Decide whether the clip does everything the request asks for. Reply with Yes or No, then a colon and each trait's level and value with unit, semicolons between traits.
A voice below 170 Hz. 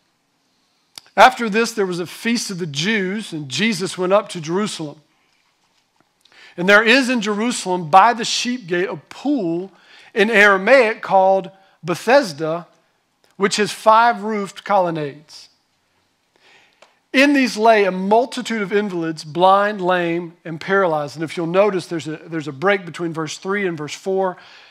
No: high, 190 Hz